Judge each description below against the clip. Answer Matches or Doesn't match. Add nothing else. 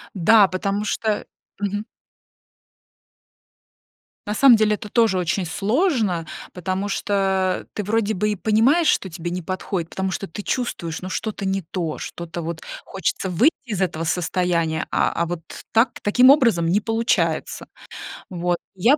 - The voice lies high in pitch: Matches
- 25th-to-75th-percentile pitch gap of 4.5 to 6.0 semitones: Doesn't match